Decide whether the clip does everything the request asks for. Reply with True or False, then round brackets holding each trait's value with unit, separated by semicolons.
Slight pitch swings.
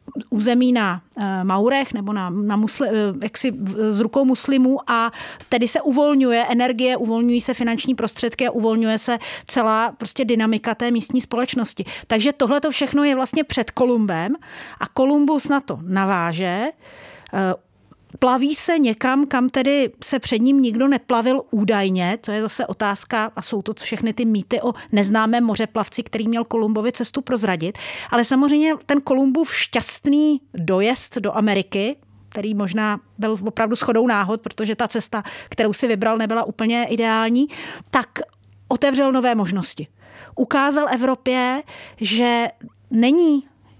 False (3.3 semitones)